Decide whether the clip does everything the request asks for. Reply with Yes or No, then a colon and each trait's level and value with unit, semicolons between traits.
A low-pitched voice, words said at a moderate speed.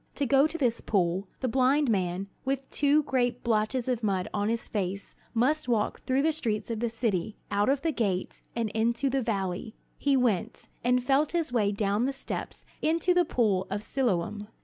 No: high, 235 Hz; average, 195 wpm